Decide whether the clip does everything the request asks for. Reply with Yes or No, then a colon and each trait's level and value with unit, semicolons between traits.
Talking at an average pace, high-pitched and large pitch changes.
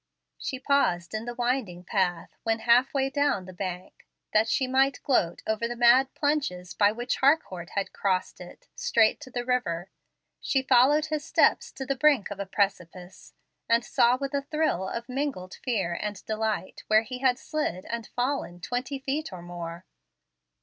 Yes: average, 175 wpm; high, 235 Hz; wide, 6.1 semitones